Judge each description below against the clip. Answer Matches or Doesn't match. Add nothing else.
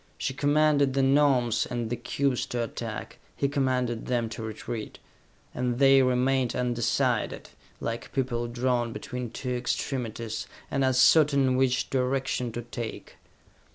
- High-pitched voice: Doesn't match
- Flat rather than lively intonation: Matches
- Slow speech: Matches